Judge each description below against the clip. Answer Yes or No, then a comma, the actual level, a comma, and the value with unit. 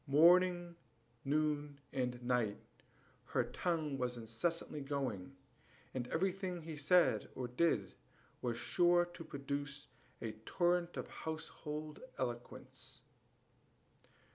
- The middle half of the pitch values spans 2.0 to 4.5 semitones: No, average, 5.3 semitones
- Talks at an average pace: No, slow, 100 wpm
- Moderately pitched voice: Yes, medium, 150 Hz